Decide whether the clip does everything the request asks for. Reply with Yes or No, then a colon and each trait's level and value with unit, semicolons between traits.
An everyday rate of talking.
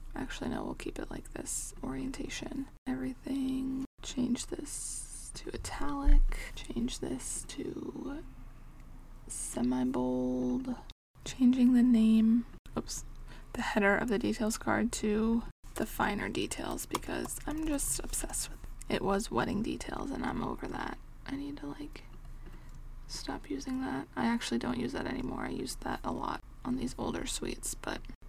Yes: average, 145 wpm